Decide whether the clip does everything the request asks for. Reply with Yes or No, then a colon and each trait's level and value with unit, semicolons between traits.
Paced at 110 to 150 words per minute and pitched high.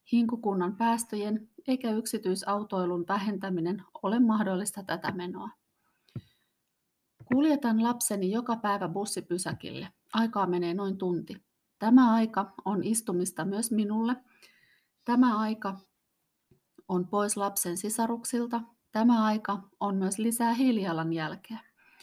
No: average, 100 wpm; high, 205 Hz